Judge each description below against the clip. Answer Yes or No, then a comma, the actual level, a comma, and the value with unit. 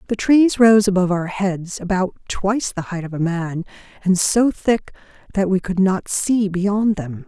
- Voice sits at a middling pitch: No, high, 195 Hz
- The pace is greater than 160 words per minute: Yes, average, 190 wpm